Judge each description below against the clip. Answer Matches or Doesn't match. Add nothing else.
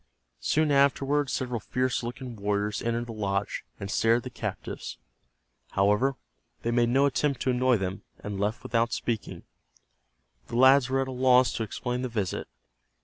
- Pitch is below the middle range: Matches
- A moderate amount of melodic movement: Matches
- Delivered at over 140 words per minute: Matches